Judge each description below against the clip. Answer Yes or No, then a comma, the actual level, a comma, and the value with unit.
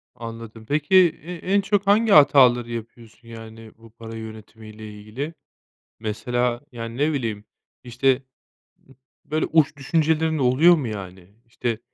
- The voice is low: Yes, low, 120 Hz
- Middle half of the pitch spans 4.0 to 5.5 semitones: Yes, average, 5.0 semitones